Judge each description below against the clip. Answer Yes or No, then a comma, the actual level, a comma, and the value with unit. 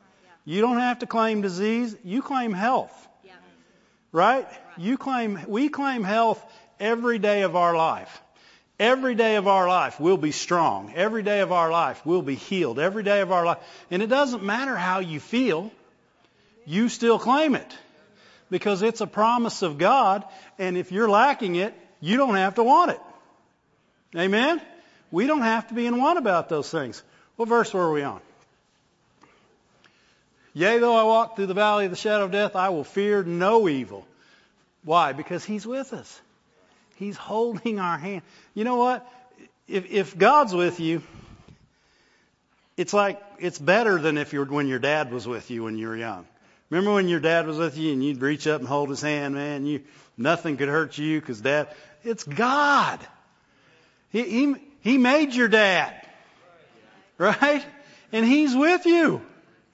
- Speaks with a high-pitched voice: Yes, high, 205 Hz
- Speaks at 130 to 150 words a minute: No, average, 175 wpm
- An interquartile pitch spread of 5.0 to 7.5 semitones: Yes, wide, 5.6 semitones